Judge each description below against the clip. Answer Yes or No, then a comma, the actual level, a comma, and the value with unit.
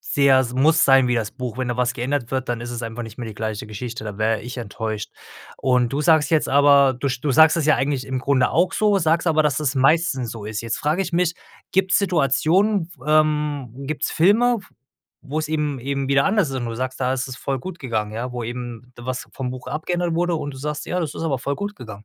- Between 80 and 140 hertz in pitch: Yes, low, 135 Hz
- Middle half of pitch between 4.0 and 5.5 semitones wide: Yes, average, 4.4 semitones